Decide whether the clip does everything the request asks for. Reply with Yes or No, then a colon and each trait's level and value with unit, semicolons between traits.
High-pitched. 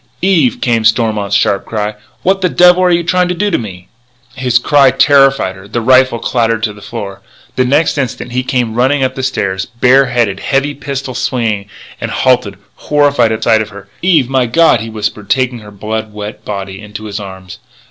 No: low, 120 Hz